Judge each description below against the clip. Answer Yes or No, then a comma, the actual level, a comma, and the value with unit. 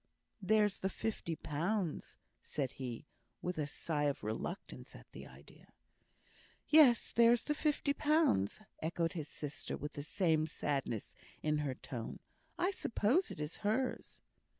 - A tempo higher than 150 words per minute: No, average, 140 wpm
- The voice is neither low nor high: Yes, medium, 165 Hz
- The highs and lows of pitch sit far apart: Yes, wide, 7.3 semitones